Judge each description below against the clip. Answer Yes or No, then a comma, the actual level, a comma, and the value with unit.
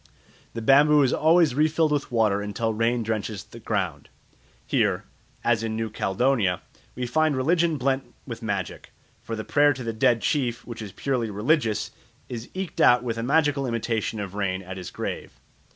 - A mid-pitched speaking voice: No, low, 115 Hz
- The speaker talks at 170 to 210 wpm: Yes, average, 175 wpm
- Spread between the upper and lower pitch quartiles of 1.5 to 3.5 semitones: No, average, 4.3 semitones